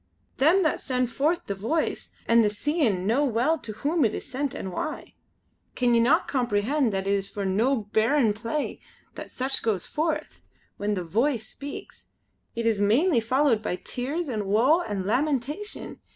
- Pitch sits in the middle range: No, high, 240 Hz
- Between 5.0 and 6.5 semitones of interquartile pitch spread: Yes, wide, 5.6 semitones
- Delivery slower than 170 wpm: No, average, 175 wpm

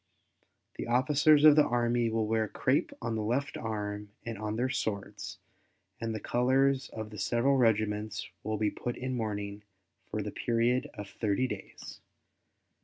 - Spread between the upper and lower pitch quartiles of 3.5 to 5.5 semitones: No, average, 3.1 semitones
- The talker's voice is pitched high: No, low, 115 Hz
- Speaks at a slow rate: No, average, 160 wpm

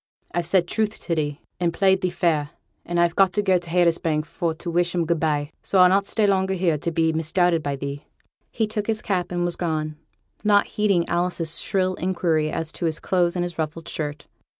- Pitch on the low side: No, medium, 175 Hz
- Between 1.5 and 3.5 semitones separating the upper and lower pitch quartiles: Yes, narrow, 2.6 semitones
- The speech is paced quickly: Yes, fast, 220 wpm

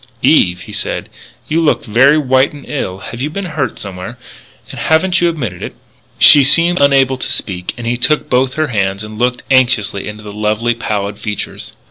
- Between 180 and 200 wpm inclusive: Yes, average, 190 wpm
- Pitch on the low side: Yes, low, 125 Hz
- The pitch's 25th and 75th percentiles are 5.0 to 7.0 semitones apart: Yes, wide, 5.6 semitones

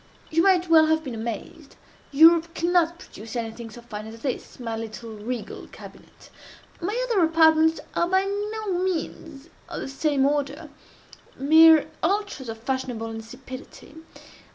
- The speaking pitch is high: Yes, very high, 305 Hz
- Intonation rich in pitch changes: Yes, wide, 6.0 semitones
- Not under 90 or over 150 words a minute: Yes, slow, 135 wpm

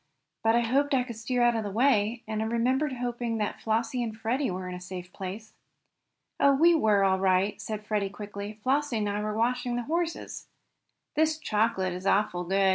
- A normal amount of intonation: Yes, average, 3.6 semitones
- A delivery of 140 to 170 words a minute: No, average, 200 wpm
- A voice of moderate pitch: No, high, 225 Hz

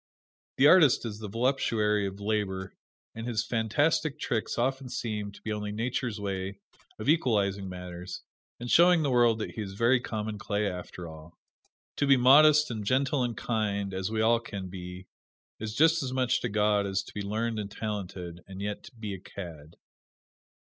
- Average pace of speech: Yes, average, 180 wpm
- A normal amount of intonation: Yes, average, 3.9 semitones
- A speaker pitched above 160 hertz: No, low, 110 Hz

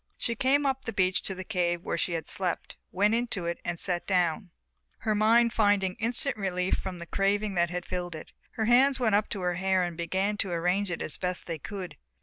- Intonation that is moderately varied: Yes, average, 3.4 semitones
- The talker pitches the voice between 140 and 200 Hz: Yes, high, 190 Hz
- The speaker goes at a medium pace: No, fast, 225 wpm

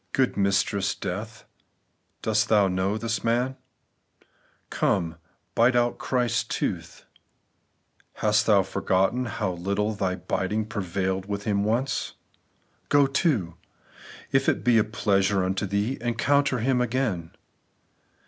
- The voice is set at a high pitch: No, low, 105 Hz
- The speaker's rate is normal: No, slow, 120 wpm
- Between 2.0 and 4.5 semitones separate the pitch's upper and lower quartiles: Yes, average, 3.6 semitones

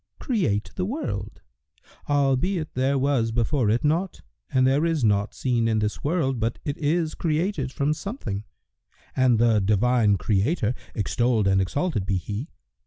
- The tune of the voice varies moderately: No, wide, 6.1 semitones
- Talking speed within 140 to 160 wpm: Yes, average, 150 wpm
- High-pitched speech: No, low, 130 Hz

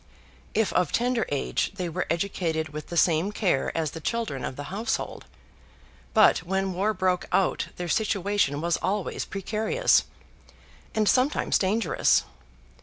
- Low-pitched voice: No, high, 190 Hz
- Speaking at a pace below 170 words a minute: Yes, average, 140 wpm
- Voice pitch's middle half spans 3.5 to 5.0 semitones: Yes, average, 4.5 semitones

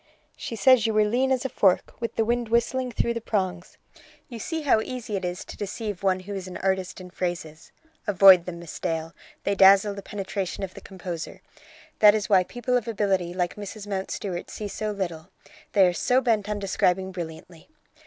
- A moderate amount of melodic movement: Yes, average, 3.4 semitones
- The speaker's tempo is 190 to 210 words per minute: Yes, average, 200 wpm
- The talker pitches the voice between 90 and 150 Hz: No, high, 195 Hz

